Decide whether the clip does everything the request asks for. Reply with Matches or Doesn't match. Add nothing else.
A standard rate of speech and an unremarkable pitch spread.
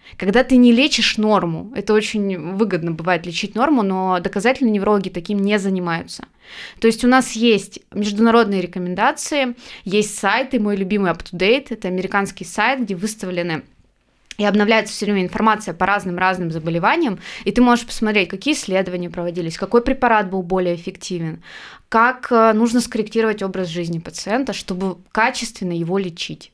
Matches